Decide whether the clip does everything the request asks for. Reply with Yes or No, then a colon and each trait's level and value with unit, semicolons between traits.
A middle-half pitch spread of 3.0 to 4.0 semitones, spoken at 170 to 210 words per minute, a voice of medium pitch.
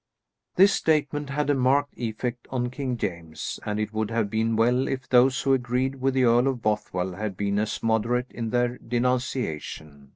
No: average, 3.3 semitones; average, 185 wpm; low, 120 Hz